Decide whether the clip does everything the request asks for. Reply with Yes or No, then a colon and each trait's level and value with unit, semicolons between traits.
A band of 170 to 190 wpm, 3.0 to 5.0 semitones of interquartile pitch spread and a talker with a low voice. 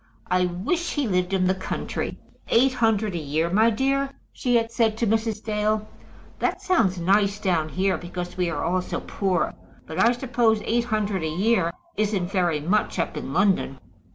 No: average, 180 wpm; average, 4.0 semitones; high, 200 Hz